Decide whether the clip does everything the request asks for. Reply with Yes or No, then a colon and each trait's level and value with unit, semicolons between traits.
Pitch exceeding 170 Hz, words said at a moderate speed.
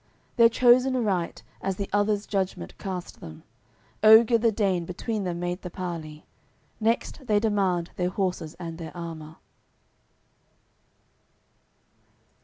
No: high, 190 Hz; slow, 120 wpm